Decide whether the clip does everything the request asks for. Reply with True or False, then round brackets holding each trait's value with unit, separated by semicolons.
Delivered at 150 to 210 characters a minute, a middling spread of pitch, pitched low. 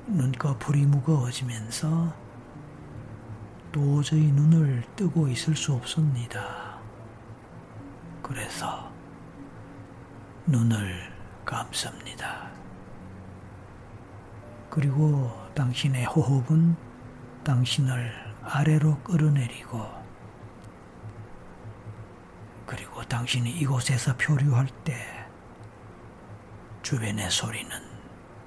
True (155 characters per minute; 4.2 semitones; 125 Hz)